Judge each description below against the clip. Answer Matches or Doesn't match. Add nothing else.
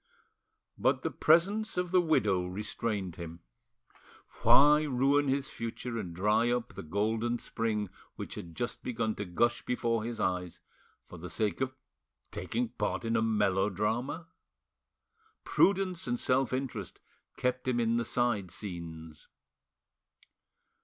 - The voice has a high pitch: Doesn't match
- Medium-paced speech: Doesn't match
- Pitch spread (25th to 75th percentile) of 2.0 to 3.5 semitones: Doesn't match